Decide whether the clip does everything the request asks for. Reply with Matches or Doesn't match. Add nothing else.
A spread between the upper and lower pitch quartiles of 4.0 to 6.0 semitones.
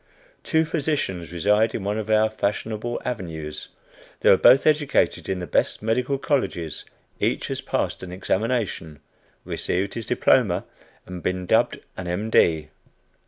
Matches